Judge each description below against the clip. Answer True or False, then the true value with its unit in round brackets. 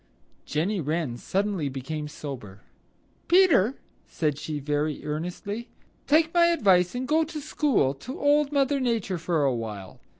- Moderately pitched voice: True (180 Hz)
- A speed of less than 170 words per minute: True (135 wpm)